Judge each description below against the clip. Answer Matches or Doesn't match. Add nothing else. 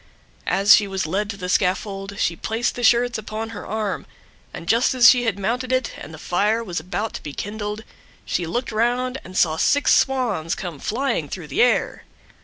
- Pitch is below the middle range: Doesn't match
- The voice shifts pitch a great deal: Doesn't match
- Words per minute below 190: Doesn't match